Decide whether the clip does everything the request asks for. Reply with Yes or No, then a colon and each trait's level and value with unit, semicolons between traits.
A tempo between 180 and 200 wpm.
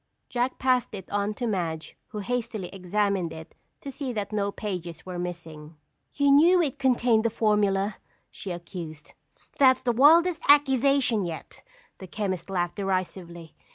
No: average, 150 wpm